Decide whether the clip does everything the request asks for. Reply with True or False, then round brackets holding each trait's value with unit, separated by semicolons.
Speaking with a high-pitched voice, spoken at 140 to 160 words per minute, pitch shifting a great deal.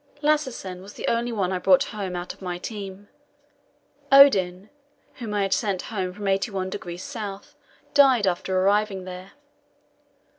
False (195 Hz; 145 wpm; 2.7 semitones)